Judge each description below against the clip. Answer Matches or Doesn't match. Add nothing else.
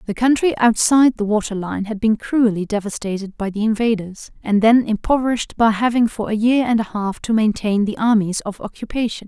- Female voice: Matches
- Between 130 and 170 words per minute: Doesn't match